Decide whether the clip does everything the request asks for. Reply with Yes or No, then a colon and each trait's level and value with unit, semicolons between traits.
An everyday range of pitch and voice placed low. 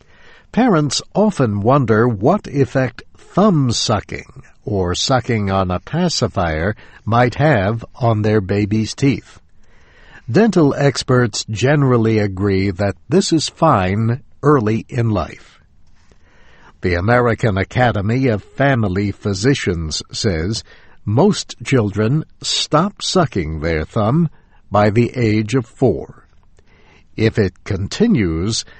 Yes: average, 4.8 semitones; low, 110 Hz